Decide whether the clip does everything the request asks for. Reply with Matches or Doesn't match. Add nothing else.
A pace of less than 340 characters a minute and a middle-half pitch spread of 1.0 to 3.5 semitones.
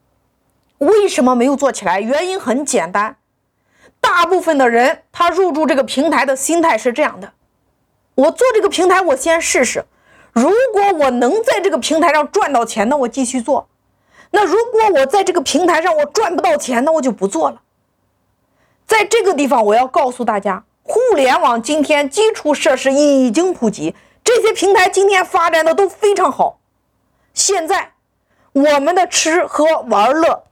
Doesn't match